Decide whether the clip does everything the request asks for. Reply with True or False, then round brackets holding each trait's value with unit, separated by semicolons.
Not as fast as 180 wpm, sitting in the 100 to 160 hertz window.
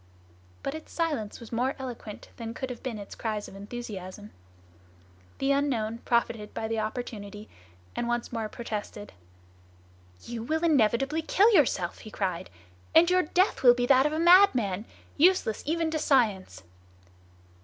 False (150 wpm; 240 Hz)